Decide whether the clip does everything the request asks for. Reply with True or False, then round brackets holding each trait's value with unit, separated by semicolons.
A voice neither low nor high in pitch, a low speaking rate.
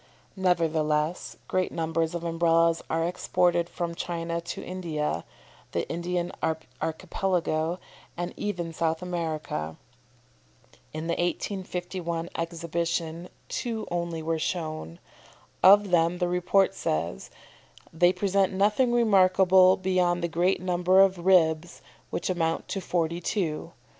True (175 Hz; 115 wpm)